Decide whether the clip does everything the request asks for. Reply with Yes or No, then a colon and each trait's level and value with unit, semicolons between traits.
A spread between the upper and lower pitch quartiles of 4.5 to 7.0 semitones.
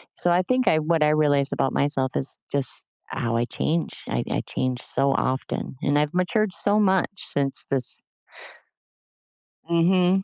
Yes: average, 4.8 semitones